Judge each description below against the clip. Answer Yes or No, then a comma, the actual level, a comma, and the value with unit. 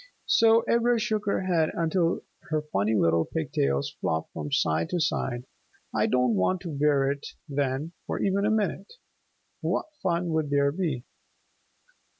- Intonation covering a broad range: Yes, wide, 6.8 semitones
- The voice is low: No, medium, 155 Hz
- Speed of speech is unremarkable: Yes, average, 155 wpm